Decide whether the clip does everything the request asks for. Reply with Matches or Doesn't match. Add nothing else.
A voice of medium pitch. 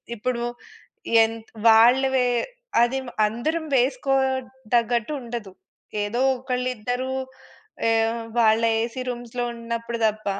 Doesn't match